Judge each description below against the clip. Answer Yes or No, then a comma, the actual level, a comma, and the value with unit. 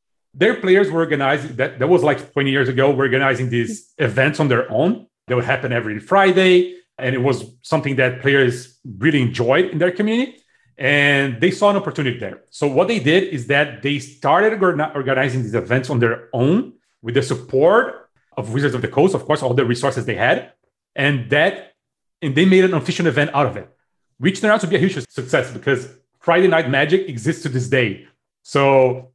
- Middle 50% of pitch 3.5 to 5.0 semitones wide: Yes, average, 4.5 semitones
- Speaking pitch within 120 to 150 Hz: Yes, medium, 140 Hz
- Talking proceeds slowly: No, average, 200 wpm